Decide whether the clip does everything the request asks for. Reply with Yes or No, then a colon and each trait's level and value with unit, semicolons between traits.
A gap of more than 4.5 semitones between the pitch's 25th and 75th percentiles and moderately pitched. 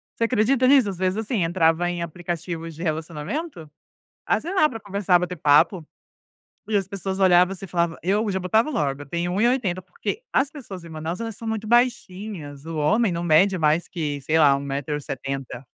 Yes: average, 5.1 semitones; medium, 180 Hz